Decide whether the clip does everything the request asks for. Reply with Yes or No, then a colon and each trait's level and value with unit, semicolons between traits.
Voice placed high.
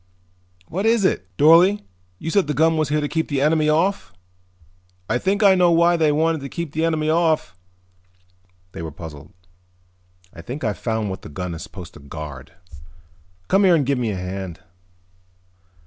No: medium, 150 Hz